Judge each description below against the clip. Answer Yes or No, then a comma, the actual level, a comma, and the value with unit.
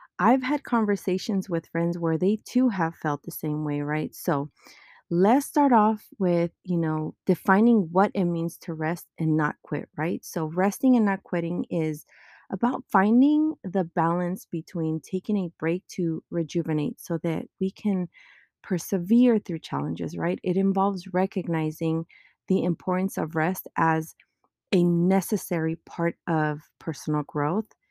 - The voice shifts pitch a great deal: No, average, 3.2 semitones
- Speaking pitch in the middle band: Yes, medium, 175 Hz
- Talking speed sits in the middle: Yes, average, 150 wpm